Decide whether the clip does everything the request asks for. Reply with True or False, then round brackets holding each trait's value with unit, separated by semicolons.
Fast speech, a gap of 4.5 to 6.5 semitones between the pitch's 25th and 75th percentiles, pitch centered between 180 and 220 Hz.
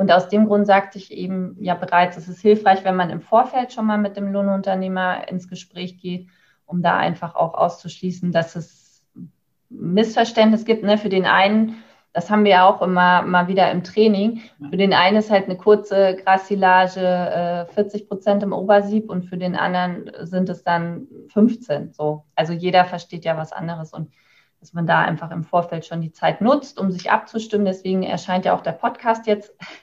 False (195 wpm; 2.8 semitones; 185 Hz)